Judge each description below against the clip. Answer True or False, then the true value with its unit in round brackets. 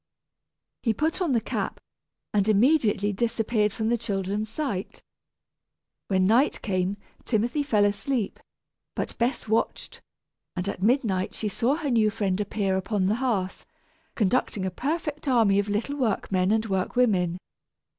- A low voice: False (215 Hz)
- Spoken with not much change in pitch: False (3.8 semitones)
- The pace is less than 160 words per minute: True (140 wpm)